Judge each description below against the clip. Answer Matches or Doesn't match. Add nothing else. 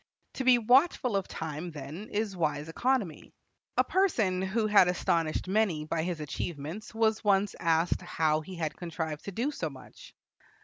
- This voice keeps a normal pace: Matches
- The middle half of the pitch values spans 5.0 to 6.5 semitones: Matches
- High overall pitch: Doesn't match